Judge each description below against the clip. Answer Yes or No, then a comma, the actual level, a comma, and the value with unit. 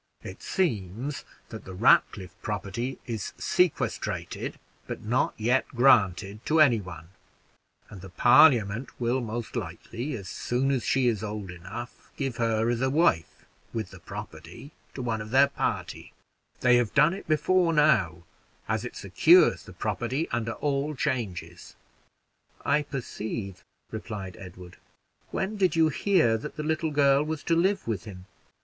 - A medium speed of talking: Yes, average, 150 wpm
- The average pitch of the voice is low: Yes, low, 120 Hz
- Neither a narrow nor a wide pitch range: No, wide, 6.1 semitones